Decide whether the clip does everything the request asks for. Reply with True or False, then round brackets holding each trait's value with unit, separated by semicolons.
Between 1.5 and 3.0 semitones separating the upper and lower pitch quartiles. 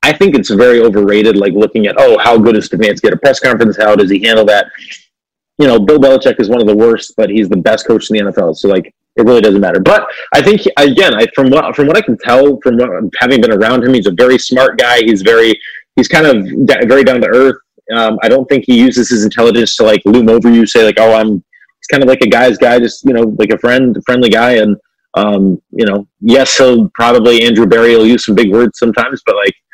True (2.5 semitones)